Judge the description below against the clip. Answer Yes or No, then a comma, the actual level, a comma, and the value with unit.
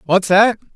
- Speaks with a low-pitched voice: No, high, 200 Hz